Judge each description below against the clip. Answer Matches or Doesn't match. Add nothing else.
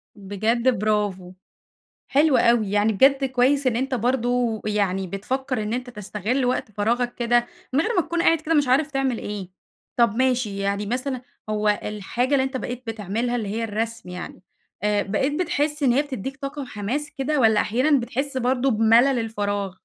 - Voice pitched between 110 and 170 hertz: Doesn't match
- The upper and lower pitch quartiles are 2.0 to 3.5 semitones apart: Doesn't match